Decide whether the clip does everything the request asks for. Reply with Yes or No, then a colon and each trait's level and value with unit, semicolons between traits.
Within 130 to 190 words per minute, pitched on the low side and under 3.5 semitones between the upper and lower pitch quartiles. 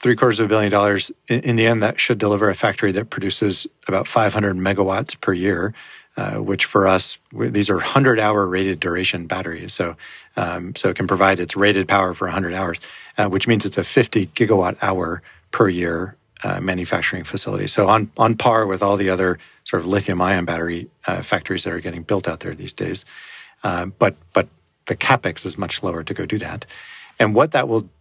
No: average, 200 wpm; low, 100 Hz; average, 2.8 semitones